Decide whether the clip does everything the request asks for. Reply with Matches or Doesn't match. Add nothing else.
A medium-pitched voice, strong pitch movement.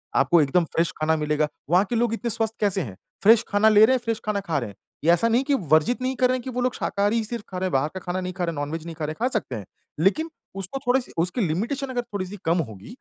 Doesn't match